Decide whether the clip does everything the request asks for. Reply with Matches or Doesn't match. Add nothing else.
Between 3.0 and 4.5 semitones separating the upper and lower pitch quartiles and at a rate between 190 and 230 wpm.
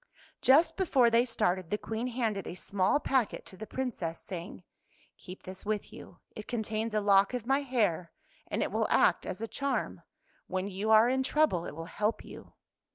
Doesn't match